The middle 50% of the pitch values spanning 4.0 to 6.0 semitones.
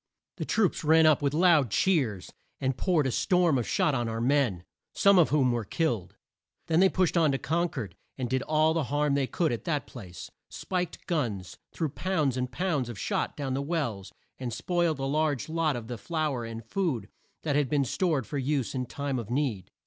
Yes: average, 4.8 semitones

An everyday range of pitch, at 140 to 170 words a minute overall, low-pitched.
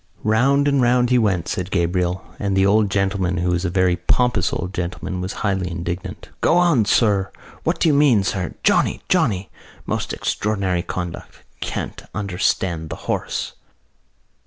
Yes: average, 3.3 semitones; average, 160 wpm; very low, 95 Hz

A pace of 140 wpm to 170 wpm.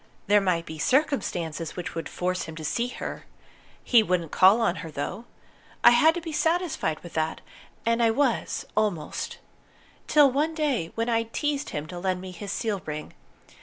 No: average, 180 wpm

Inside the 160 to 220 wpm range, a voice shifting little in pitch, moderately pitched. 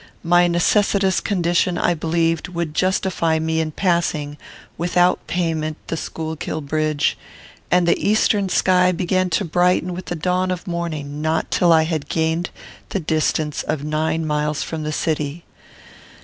No: average, 150 wpm; narrow, 2.3 semitones; medium, 165 Hz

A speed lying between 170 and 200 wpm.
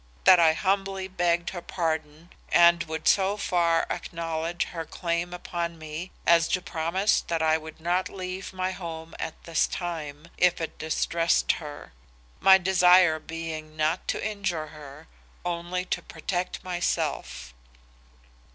No: average, 140 wpm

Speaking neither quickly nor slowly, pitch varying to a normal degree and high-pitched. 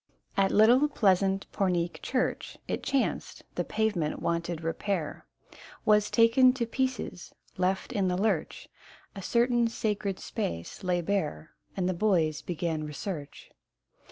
No: slow, 130 wpm; average, 4.5 semitones; high, 195 Hz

